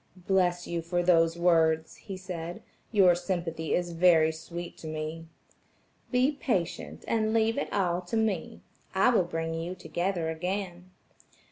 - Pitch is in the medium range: Yes, medium, 175 Hz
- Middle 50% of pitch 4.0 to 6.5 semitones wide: No, narrow, 2.6 semitones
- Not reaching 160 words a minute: Yes, average, 145 wpm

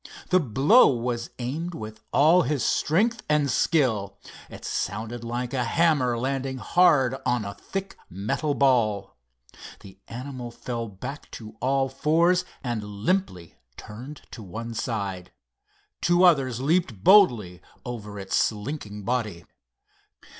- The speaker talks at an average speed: No, slow, 125 wpm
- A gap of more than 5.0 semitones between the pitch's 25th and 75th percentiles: Yes, wide, 5.5 semitones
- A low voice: Yes, low, 125 Hz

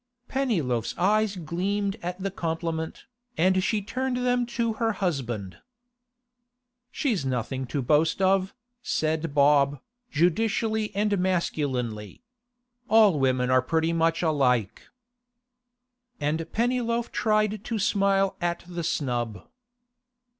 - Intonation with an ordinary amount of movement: No, wide, 6.7 semitones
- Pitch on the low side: No, medium, 175 Hz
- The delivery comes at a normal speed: No, slow, 110 wpm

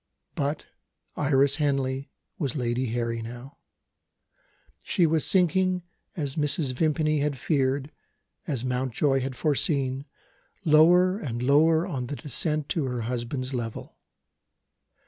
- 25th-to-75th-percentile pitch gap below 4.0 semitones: Yes, average, 3.2 semitones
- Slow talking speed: Yes, slow, 115 wpm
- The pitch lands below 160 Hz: Yes, medium, 140 Hz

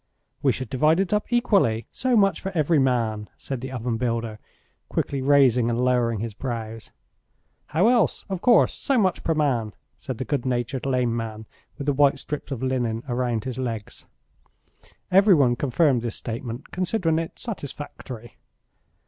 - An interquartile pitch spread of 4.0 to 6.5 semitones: Yes, average, 5.2 semitones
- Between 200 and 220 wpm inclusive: No, average, 165 wpm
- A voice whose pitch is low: Yes, low, 130 Hz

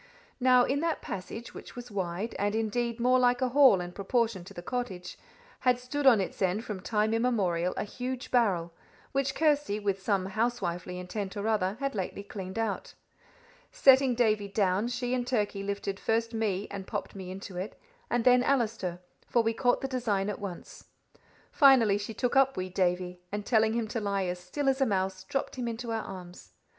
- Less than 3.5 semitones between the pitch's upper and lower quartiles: No, average, 4.4 semitones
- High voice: Yes, high, 215 Hz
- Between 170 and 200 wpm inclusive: Yes, average, 195 wpm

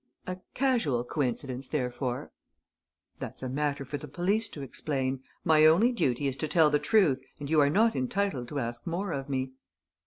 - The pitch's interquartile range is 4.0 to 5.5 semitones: Yes, average, 4.8 semitones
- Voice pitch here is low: No, medium, 145 Hz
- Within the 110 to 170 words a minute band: No, average, 180 wpm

